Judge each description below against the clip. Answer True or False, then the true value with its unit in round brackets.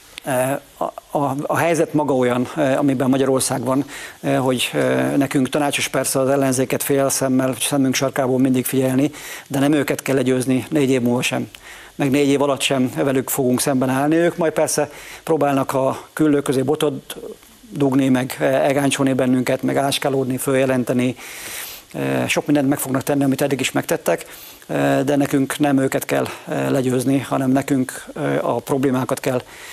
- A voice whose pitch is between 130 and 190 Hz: True (135 Hz)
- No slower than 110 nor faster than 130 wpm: False (150 wpm)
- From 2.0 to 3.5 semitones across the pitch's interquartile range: False (1.6 semitones)